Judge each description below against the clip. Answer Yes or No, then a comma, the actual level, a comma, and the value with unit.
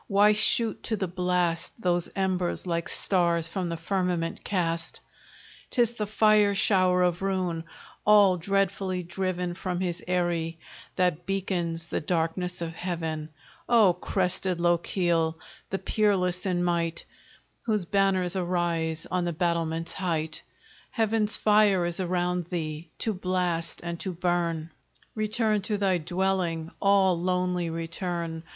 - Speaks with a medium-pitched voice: Yes, medium, 180 Hz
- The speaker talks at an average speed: No, slow, 130 wpm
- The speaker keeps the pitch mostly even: Yes, narrow, 2.3 semitones